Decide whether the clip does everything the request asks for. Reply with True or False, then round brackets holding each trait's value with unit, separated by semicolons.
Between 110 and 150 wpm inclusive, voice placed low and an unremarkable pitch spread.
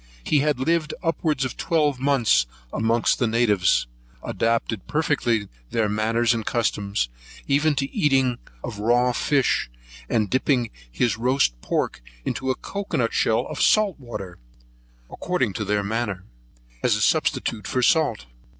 True (140 wpm; 120 Hz; 4.5 semitones)